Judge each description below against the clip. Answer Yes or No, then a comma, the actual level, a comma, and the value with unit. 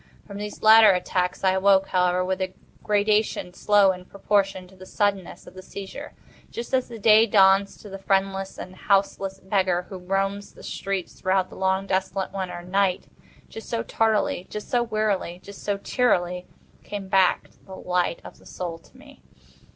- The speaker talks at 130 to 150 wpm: No, average, 165 wpm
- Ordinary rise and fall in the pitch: No, narrow, 1.7 semitones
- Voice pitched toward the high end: Yes, high, 195 Hz